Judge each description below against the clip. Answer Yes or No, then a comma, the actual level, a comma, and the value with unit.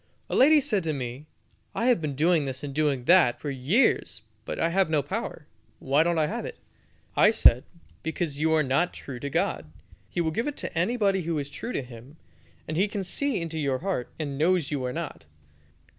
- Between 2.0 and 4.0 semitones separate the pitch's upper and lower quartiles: No, average, 4.9 semitones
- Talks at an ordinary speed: No, fast, 215 wpm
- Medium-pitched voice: Yes, medium, 160 Hz